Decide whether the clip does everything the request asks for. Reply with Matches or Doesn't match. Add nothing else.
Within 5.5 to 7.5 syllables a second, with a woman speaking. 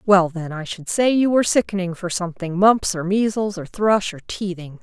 Doesn't match